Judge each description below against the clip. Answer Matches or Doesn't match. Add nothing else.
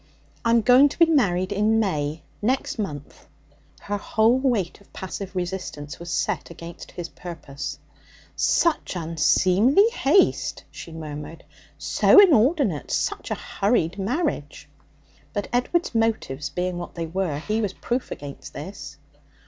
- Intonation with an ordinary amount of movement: Doesn't match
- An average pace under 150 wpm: Matches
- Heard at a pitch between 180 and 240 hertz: Matches